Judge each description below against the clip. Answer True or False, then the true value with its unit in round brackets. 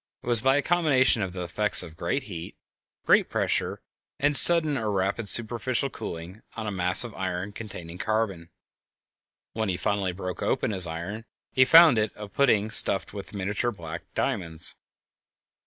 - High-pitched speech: False (105 Hz)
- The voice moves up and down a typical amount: True (4.7 semitones)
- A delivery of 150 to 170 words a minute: True (165 wpm)